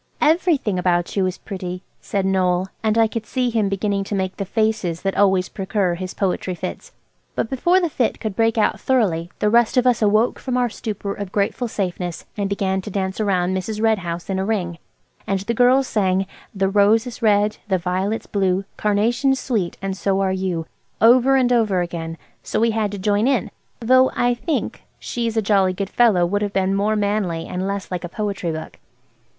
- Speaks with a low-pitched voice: No, high, 200 Hz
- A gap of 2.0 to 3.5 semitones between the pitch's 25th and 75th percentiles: Yes, average, 3.2 semitones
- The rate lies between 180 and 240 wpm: Yes, average, 200 wpm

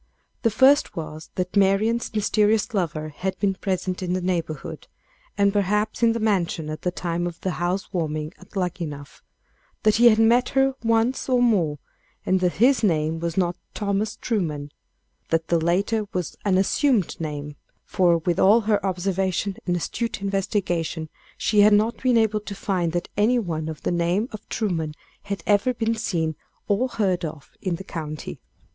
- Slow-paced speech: No, average, 175 wpm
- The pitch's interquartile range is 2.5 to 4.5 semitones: Yes, average, 4.1 semitones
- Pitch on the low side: No, high, 190 Hz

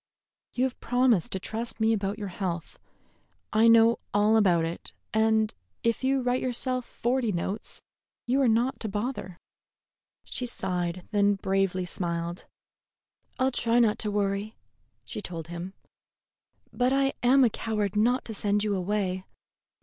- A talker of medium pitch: No, high, 215 Hz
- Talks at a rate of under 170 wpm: Yes, average, 150 wpm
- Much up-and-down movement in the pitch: No, average, 4.0 semitones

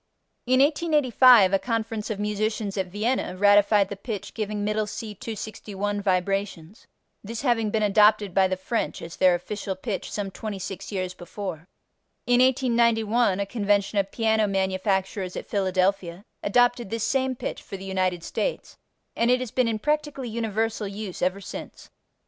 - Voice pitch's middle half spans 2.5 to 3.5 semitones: Yes, average, 3.0 semitones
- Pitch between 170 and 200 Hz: No, high, 210 Hz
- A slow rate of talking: No, average, 155 wpm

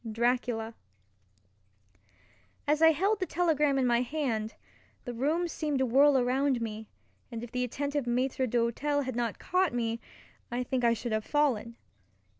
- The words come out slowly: No, average, 155 wpm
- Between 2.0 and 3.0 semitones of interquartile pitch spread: No, average, 3.8 semitones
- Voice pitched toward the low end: No, very high, 250 Hz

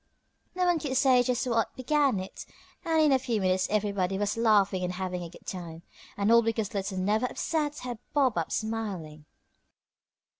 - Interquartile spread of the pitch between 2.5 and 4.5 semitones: No, average, 5.2 semitones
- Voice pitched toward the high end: Yes, high, 215 Hz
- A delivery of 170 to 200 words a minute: Yes, average, 180 wpm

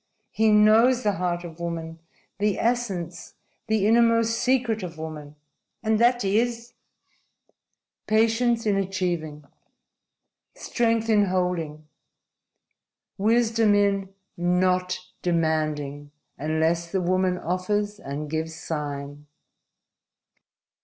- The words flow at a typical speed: No, slow, 100 wpm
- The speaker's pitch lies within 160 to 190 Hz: Yes, medium, 185 Hz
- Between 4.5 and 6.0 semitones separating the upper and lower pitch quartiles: Yes, average, 5.3 semitones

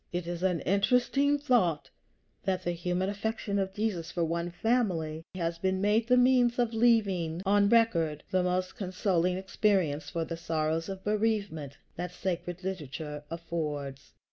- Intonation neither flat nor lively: Yes, average, 4.0 semitones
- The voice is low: No, medium, 185 Hz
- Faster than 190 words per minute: No, average, 150 wpm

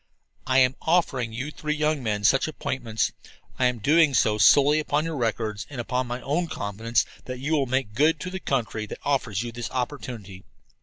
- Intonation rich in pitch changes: No, average, 4.6 semitones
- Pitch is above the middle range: No, low, 130 Hz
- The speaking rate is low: No, average, 195 wpm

